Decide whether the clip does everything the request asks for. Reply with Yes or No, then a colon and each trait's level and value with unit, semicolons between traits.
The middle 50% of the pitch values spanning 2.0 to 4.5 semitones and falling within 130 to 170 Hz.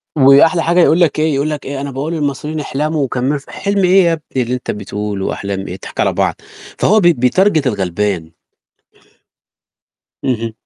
No: wide, 5.6 semitones; medium, 140 Hz